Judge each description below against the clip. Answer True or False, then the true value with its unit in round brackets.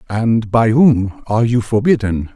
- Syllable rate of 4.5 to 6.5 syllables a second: False (4.3 syllables/s)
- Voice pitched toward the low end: True (115 Hz)